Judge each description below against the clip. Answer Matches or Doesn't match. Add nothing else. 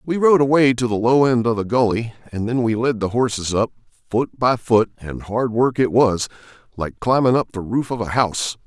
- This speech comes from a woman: Doesn't match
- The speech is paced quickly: Matches